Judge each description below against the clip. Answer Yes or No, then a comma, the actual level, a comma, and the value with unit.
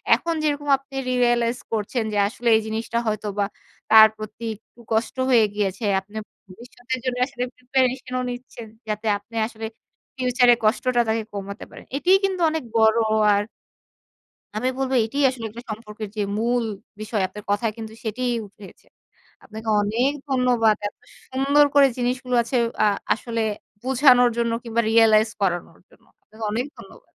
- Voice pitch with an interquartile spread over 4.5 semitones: No, average, 2.7 semitones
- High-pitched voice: Yes, high, 235 Hz